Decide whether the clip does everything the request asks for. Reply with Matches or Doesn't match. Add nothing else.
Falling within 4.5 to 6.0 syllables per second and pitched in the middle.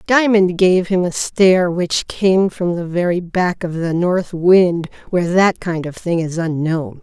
Doesn't match